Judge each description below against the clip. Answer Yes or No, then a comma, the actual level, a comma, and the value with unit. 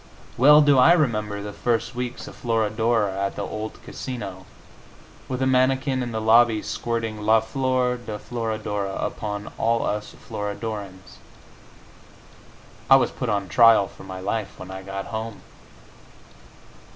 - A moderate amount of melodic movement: Yes, average, 3.2 semitones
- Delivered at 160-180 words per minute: No, average, 140 wpm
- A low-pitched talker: Yes, low, 110 Hz